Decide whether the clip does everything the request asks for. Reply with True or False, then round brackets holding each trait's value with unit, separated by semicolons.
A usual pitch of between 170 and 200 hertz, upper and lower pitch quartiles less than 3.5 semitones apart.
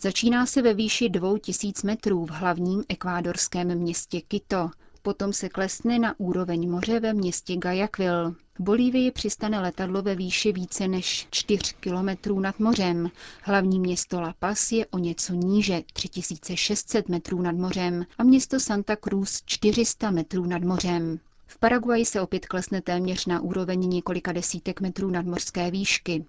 True (185 Hz; 2.8 semitones)